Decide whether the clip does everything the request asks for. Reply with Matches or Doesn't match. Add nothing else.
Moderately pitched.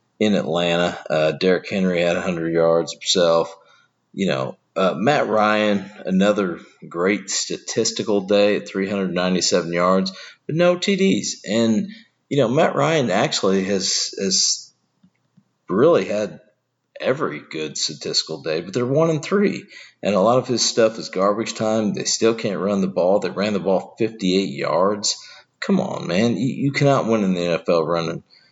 Doesn't match